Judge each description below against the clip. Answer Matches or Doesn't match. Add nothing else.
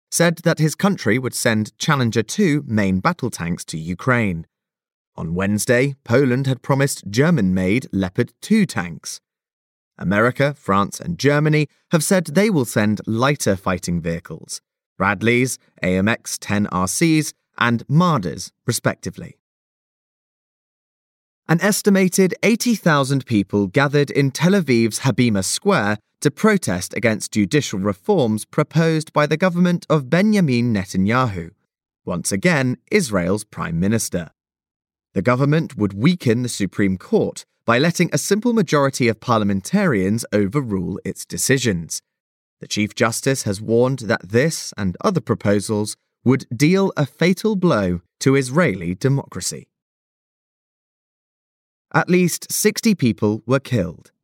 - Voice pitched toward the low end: Matches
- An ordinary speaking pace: Doesn't match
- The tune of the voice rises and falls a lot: Matches